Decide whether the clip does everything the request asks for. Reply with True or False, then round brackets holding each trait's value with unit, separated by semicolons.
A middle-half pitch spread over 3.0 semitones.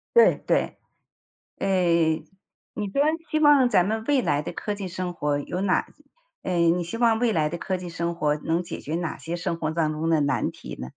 True (3.7 semitones)